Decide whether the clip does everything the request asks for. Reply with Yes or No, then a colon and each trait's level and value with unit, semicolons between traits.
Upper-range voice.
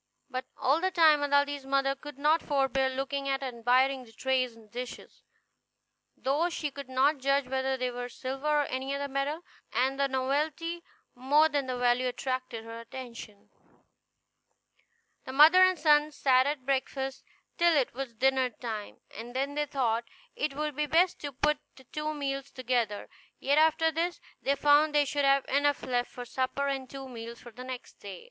Yes: very high, 270 Hz